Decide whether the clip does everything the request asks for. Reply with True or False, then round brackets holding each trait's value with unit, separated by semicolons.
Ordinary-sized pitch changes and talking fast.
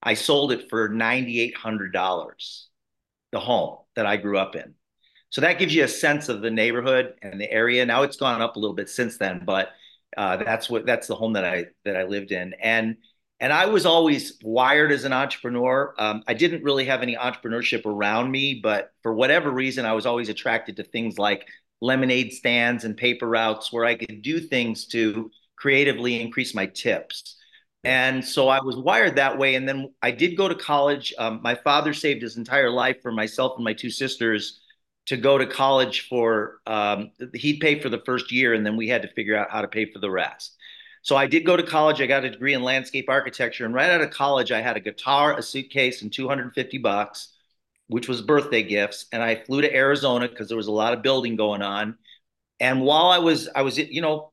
True (3.5 semitones; 215 wpm)